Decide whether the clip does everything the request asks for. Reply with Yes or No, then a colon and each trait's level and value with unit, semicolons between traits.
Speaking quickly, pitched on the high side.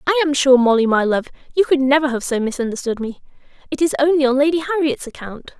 Yes: fast, 215 wpm; very high, 280 Hz